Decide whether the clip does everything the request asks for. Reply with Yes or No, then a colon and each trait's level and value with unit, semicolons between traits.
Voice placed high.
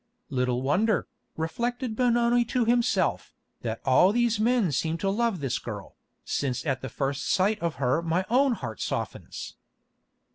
No: medium, 180 Hz